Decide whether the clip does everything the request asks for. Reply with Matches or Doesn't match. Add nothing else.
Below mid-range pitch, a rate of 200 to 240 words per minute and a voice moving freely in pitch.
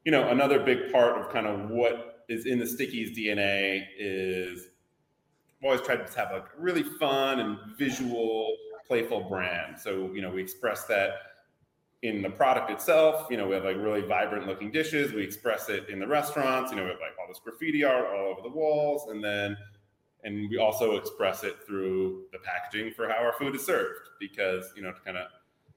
Matches